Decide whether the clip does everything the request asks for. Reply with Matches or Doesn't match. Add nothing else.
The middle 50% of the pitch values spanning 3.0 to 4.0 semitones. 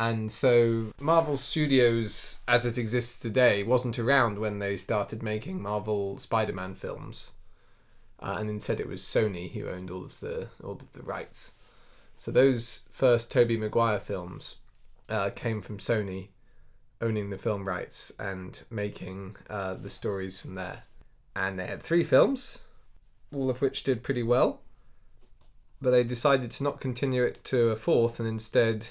Matches